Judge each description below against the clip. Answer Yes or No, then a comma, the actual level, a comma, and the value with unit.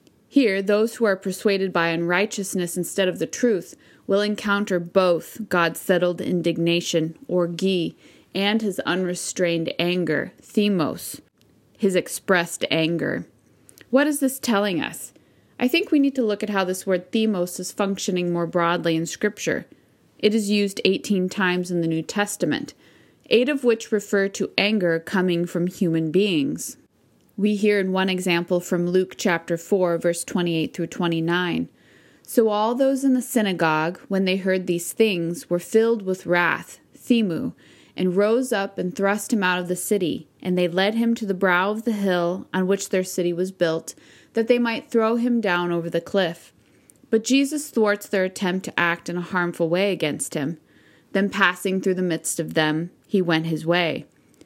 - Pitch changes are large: No, average, 3.3 semitones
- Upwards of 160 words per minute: Yes, average, 170 wpm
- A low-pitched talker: No, medium, 185 Hz